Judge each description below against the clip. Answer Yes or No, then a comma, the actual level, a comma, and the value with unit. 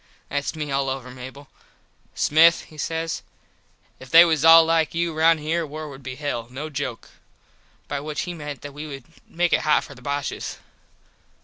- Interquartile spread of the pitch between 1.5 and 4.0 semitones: Yes, average, 2.8 semitones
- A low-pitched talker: No, medium, 150 Hz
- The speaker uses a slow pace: No, average, 185 wpm